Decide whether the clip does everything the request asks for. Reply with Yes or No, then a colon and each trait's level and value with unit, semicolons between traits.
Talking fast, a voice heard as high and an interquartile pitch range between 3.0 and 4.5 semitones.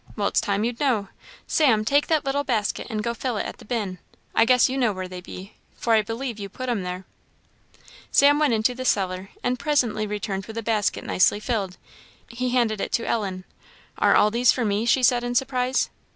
Yes: fast, 215 wpm; high, 225 Hz; average, 3.6 semitones